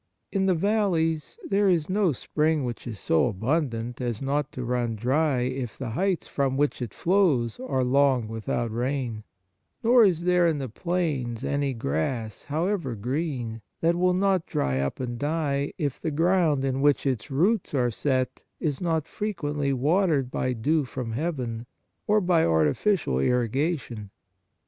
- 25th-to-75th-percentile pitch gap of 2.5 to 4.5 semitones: No, wide, 5.6 semitones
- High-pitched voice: No, medium, 140 Hz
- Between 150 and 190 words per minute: Yes, average, 160 wpm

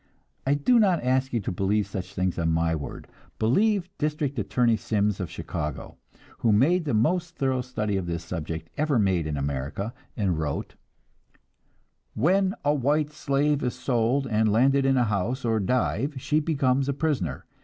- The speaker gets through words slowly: No, average, 170 wpm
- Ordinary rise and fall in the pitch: No, wide, 6.8 semitones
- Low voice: Yes, low, 125 Hz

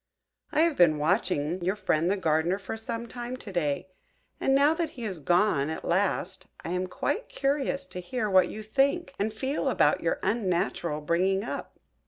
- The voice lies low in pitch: No, high, 195 Hz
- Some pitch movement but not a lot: No, wide, 6.0 semitones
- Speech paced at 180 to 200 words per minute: Yes, average, 185 wpm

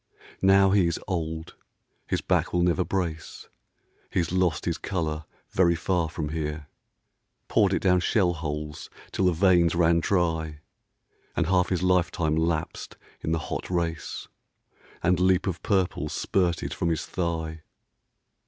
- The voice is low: Yes, very low, 85 Hz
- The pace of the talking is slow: No, average, 145 wpm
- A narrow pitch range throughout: Yes, narrow, 2.3 semitones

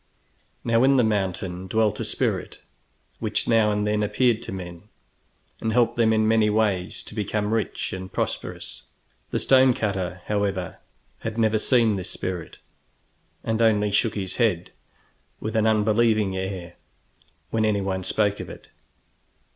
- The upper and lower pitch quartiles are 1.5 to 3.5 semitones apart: Yes, average, 2.7 semitones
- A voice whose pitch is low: Yes, low, 105 Hz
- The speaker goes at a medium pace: Yes, average, 145 wpm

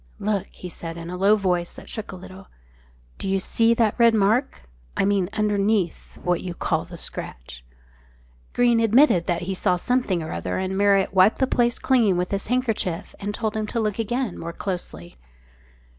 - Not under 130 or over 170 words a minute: No, average, 185 wpm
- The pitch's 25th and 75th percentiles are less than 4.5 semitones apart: Yes, average, 3.8 semitones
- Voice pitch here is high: Yes, high, 195 Hz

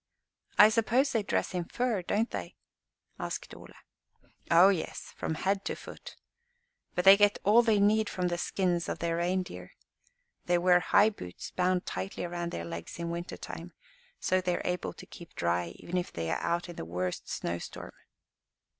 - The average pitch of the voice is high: No, medium, 180 Hz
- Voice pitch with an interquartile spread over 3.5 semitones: No, average, 3.0 semitones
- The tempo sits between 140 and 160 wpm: No, average, 180 wpm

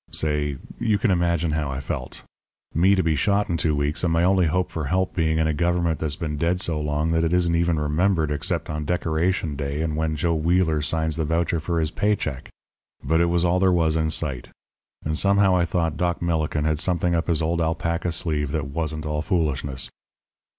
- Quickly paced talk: Yes, fast, 215 wpm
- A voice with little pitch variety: Yes, narrow, 2.2 semitones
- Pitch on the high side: No, very low, 80 Hz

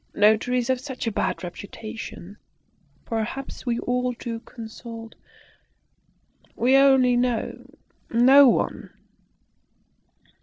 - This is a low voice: No, high, 240 Hz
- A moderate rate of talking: No, slow, 90 wpm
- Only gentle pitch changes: Yes, narrow, 2.1 semitones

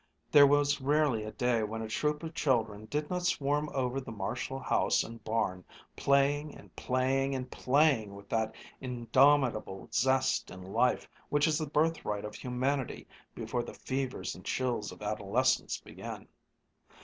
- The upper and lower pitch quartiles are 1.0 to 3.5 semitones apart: No, average, 4.4 semitones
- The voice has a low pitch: Yes, low, 130 Hz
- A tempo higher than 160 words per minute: No, average, 155 wpm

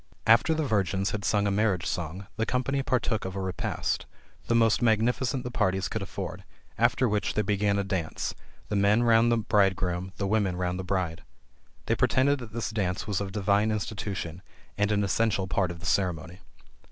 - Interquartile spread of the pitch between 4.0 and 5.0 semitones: No, average, 3.0 semitones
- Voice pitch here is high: No, low, 100 Hz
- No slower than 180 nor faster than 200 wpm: Yes, average, 190 wpm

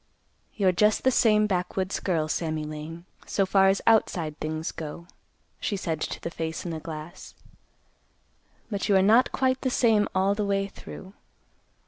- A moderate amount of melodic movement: Yes, average, 4.3 semitones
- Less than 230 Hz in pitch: Yes, high, 190 Hz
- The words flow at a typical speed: Yes, average, 165 wpm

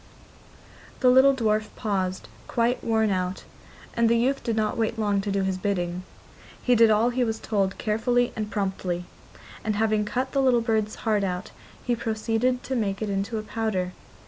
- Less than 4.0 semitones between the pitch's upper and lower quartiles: Yes, average, 2.9 semitones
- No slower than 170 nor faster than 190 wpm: Yes, average, 180 wpm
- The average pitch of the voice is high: Yes, high, 220 Hz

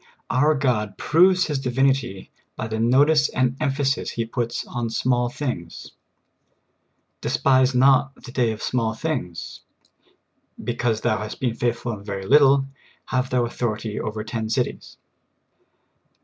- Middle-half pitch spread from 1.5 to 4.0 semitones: Yes, average, 3.4 semitones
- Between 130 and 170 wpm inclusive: Yes, average, 160 wpm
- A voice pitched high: No, low, 125 Hz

